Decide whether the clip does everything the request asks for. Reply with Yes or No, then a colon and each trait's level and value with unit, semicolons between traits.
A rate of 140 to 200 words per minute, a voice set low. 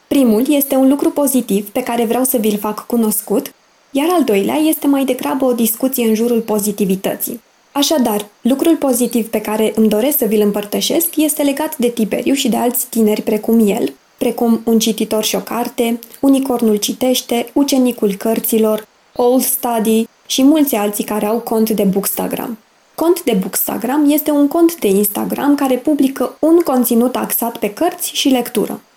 No: average, 165 wpm; high, 240 Hz